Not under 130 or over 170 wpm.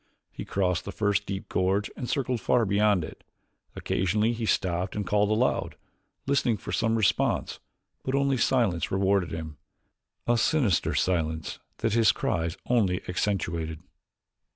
Yes: average, 140 wpm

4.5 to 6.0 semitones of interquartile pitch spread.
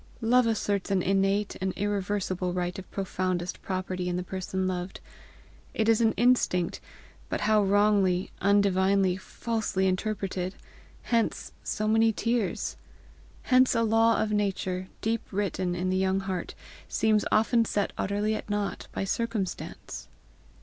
No: average, 2.7 semitones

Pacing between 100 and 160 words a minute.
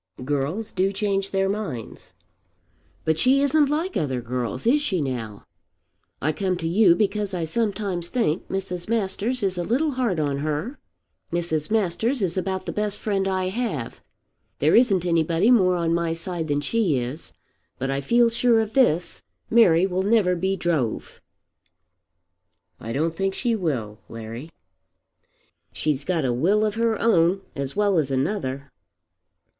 Yes: average, 155 wpm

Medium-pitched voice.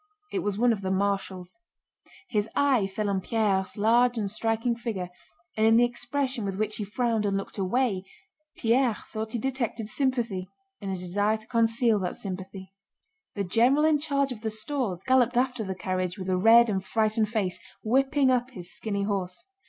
No: high, 220 Hz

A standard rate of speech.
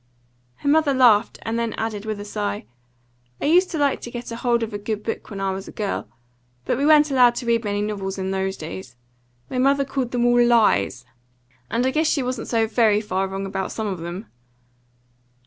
No: fast, 215 wpm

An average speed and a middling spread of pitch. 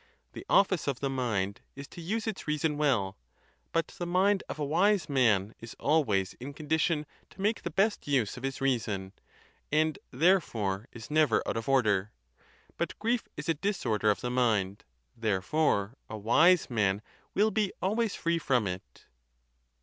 No: average, 170 wpm; wide, 7.6 semitones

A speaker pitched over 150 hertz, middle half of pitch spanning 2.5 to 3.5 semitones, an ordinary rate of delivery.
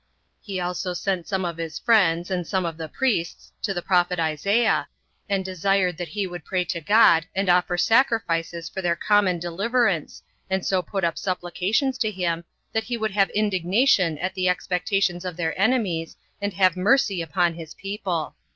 Yes: medium, 185 Hz; average, 2.9 semitones; average, 180 wpm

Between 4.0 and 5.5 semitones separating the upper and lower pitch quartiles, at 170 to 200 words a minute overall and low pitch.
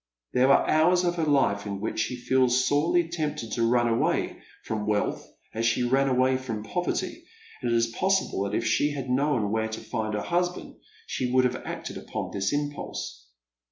Yes: average, 4.7 semitones; average, 195 wpm; low, 125 Hz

